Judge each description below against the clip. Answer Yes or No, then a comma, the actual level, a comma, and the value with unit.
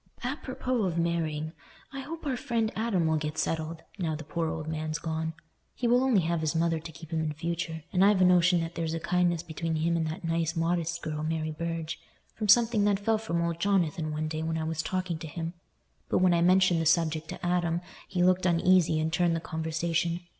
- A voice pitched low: No, medium, 170 Hz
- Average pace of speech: No, fast, 220 wpm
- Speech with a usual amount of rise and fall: No, narrow, 2.2 semitones